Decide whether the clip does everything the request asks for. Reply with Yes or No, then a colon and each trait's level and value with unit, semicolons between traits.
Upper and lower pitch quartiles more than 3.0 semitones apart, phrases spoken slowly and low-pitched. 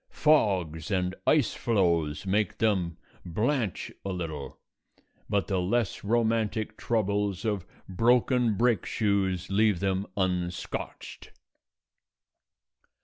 Yes: average, 3.6 semitones; slow, 95 wpm; low, 100 Hz